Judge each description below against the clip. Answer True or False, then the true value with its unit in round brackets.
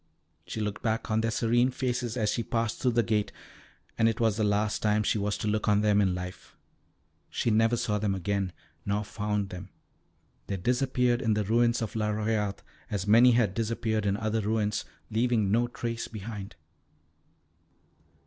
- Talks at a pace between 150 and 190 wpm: True (175 wpm)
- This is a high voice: False (110 Hz)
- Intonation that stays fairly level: True (2.0 semitones)